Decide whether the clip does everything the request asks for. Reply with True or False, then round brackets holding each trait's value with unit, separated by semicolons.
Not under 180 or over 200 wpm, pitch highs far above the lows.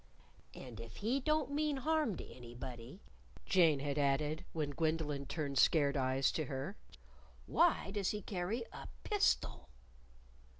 False (135 wpm; 7.6 semitones)